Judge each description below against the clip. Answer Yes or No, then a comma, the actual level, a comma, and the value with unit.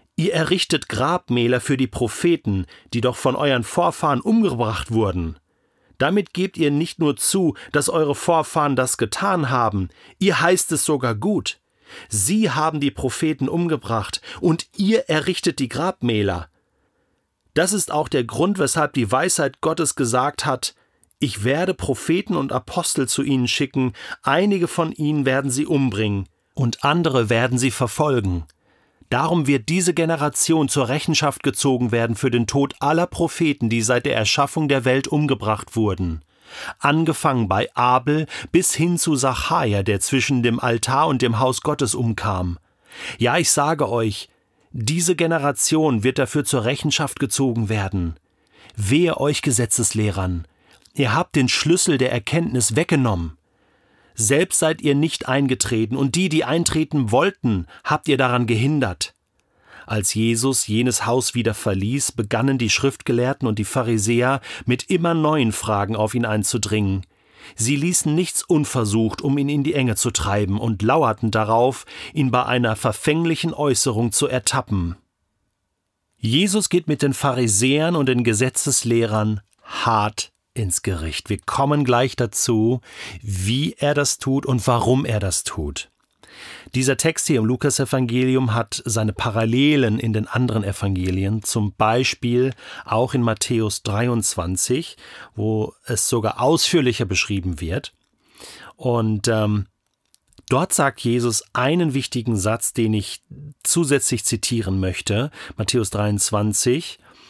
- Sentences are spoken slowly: No, average, 140 wpm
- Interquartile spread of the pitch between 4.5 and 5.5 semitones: Yes, average, 5.0 semitones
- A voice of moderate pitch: No, low, 125 Hz